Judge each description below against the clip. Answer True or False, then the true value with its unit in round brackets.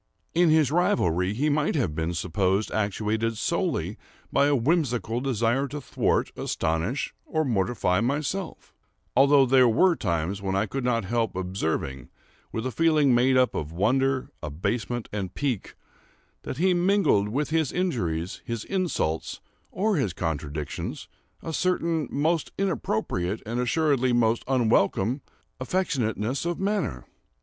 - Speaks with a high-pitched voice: False (120 Hz)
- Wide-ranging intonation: True (7.4 semitones)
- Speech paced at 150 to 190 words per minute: False (135 wpm)